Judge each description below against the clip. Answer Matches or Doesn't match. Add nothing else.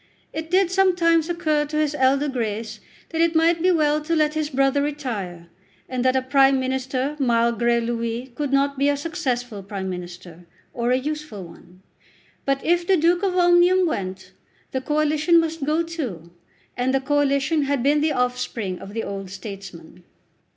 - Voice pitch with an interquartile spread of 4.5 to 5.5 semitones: Matches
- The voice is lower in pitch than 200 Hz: Doesn't match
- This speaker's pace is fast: Doesn't match